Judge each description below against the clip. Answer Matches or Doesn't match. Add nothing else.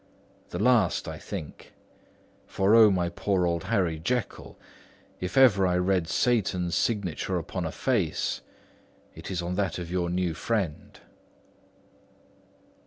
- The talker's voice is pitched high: Doesn't match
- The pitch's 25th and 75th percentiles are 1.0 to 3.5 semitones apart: Matches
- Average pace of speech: Doesn't match